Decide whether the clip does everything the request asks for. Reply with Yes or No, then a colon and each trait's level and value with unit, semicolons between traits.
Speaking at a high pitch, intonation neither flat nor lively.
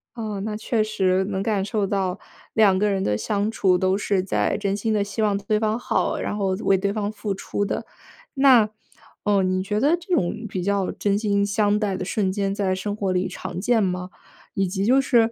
No: high, 200 Hz; narrow, 2.0 semitones